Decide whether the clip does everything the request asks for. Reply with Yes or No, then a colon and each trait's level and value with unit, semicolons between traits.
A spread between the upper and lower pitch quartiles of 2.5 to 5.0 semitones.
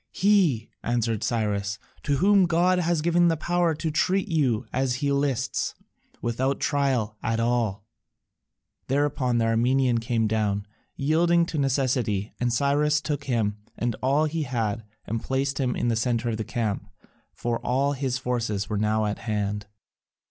Yes: average, 4.6 semitones